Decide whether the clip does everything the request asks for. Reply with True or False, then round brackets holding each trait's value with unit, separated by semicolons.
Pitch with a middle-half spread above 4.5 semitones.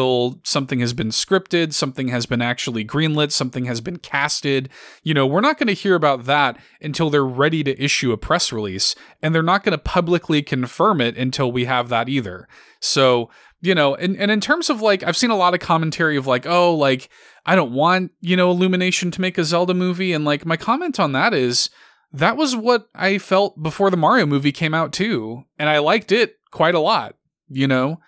True (5.5 semitones)